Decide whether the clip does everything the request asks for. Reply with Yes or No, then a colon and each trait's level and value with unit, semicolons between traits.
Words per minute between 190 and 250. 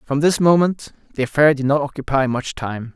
Yes: fast, 205 wpm